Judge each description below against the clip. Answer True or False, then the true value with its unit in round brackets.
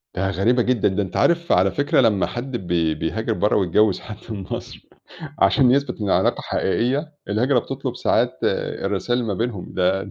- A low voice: True (105 Hz)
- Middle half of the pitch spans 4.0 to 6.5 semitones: True (4.5 semitones)